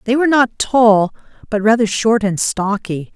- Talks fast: No, average, 170 wpm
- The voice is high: Yes, high, 220 Hz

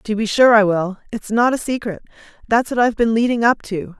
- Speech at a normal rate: No, fast, 240 wpm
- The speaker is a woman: Yes, female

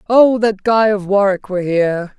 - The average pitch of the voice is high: Yes, high, 200 Hz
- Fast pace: No, average, 190 wpm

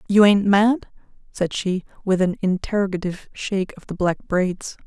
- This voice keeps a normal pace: Yes, average, 160 wpm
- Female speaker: Yes, female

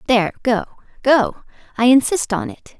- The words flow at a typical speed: No, slow, 130 wpm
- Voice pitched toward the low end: No, high, 245 Hz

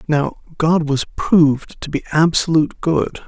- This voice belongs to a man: Yes, male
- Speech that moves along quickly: No, average, 145 wpm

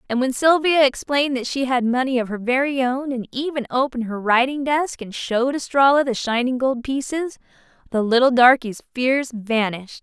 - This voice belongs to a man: No, female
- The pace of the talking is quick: No, average, 180 wpm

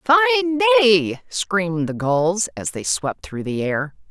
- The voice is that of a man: No, female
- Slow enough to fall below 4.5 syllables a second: Yes, 4.0 syllables/s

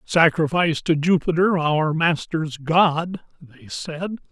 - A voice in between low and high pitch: Yes, medium, 160 Hz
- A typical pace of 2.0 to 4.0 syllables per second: Yes, 3.7 syllables/s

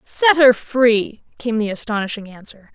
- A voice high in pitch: Yes, high, 230 Hz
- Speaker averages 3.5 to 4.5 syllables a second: Yes, 4.4 syllables/s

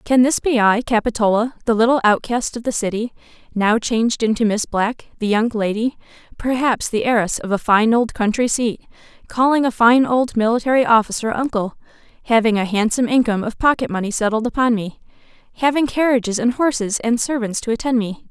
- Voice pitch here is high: Yes, high, 230 Hz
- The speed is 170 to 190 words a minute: Yes, average, 175 wpm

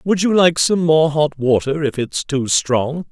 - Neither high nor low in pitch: Yes, medium, 150 Hz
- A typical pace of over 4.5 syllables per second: No, 4.0 syllables/s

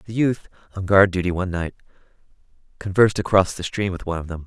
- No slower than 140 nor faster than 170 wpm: No, average, 200 wpm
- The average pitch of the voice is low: Yes, very low, 95 Hz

